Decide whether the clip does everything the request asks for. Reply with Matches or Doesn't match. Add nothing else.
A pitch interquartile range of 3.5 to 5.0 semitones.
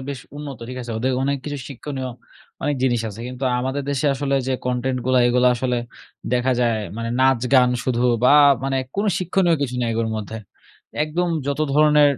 Doesn't match